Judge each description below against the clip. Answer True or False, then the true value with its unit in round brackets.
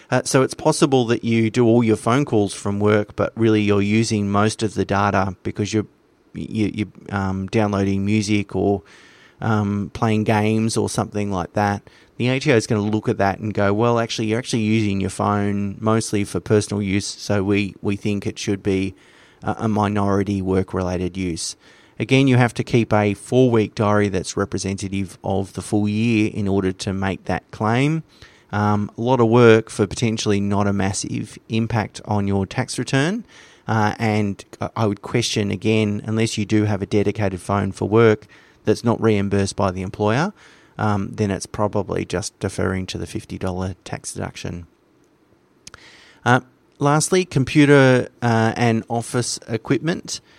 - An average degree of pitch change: False (2.3 semitones)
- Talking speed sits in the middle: True (170 wpm)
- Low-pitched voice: True (105 Hz)